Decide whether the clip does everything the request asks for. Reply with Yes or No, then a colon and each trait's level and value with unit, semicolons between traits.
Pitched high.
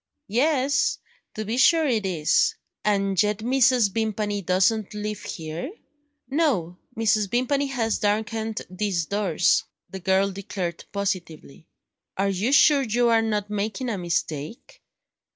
Yes: high, 210 Hz